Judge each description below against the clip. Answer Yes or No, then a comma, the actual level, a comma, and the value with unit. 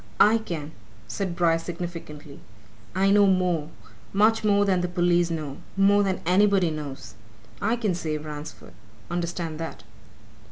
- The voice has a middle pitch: Yes, medium, 175 Hz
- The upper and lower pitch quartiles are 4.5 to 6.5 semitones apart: No, average, 3.6 semitones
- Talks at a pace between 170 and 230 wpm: No, slow, 135 wpm